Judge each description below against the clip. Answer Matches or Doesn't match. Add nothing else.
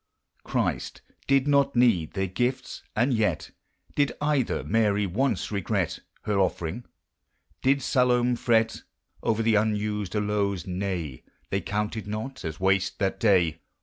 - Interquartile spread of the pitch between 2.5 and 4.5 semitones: Matches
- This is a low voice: Matches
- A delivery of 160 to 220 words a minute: Doesn't match